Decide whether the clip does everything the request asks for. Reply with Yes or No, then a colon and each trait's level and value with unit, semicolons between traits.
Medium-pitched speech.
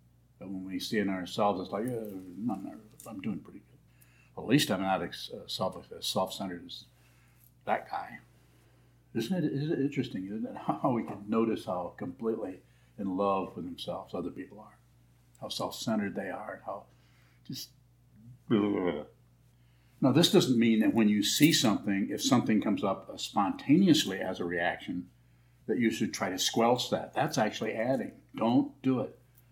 No: low, 100 Hz